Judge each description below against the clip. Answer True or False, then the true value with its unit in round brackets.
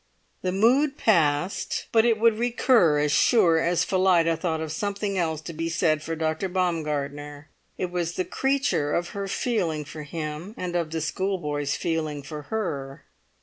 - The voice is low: False (165 Hz)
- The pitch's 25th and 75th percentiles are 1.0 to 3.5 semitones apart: False (4.3 semitones)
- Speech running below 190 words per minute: True (165 wpm)